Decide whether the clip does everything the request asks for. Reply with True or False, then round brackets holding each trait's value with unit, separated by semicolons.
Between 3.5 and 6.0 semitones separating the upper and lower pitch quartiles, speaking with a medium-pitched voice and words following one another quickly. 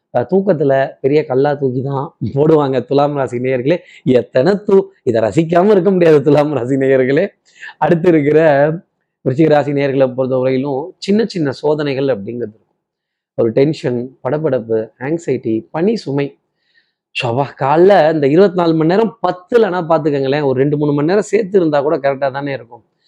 True (4.4 semitones; 145 Hz; 145 wpm)